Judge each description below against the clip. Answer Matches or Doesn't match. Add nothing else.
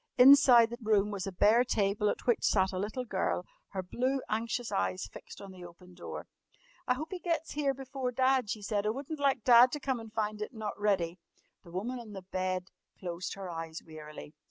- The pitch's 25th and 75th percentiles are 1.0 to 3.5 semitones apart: Doesn't match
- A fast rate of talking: Matches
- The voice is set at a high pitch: Matches